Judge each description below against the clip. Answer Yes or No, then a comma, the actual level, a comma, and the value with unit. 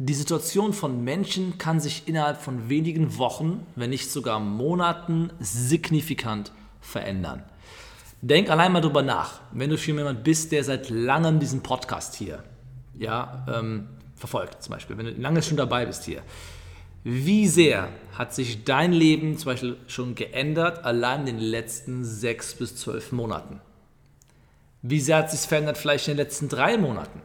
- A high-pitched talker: No, low, 130 Hz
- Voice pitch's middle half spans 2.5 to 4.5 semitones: No, average, 5.0 semitones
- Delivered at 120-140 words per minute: No, average, 160 wpm